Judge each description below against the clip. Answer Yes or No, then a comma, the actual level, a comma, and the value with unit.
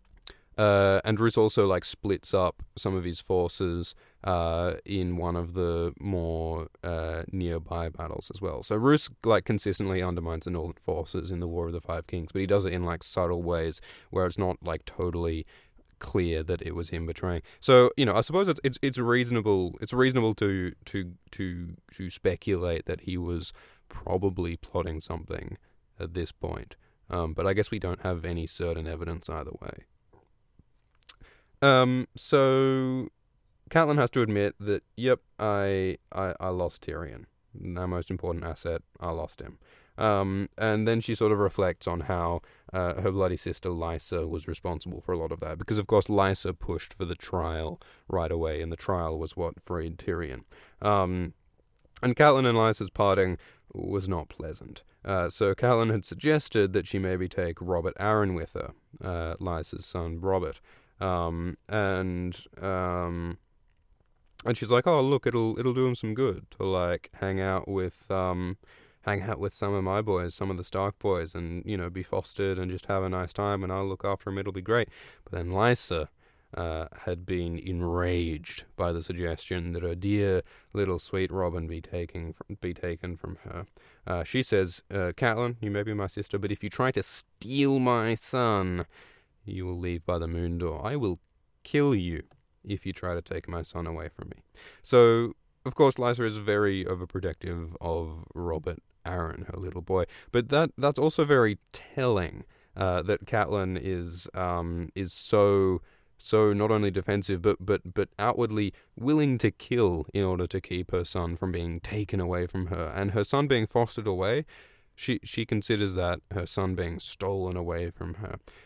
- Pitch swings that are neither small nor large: Yes, average, 3.3 semitones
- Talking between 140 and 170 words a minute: No, average, 180 wpm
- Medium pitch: No, very low, 95 Hz